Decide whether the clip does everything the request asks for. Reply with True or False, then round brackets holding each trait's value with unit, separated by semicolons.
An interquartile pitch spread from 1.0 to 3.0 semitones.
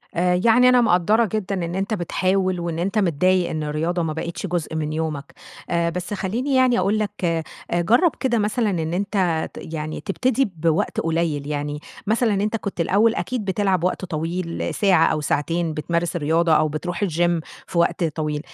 False (4.0 semitones)